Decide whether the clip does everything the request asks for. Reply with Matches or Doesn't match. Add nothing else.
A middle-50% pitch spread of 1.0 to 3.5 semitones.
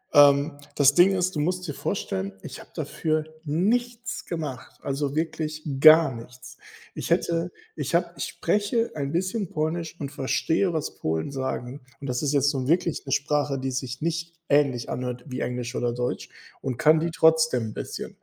Doesn't match